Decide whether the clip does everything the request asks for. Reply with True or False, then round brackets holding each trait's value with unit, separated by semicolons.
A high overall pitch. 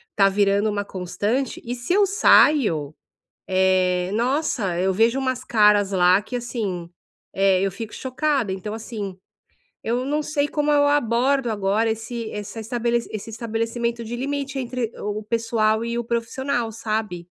True (225 Hz)